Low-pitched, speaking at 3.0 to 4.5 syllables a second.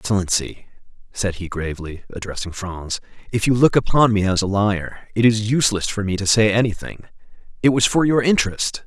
No: low, 105 Hz; 5.5 syllables/s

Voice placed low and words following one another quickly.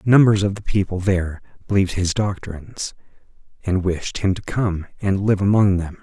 No: very low, 95 Hz; average, 170 wpm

